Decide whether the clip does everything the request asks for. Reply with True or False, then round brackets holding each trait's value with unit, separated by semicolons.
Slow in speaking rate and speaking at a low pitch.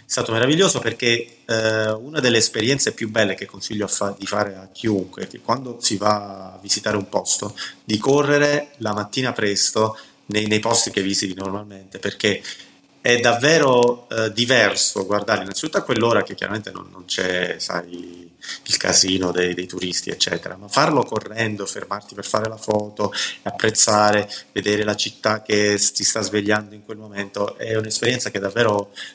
False (170 wpm; 105 Hz)